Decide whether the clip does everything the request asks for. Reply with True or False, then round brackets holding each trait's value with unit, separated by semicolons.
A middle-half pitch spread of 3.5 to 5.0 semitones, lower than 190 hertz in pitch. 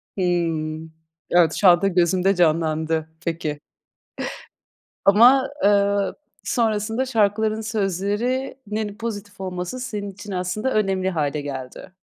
False (3.8 semitones; 195 Hz)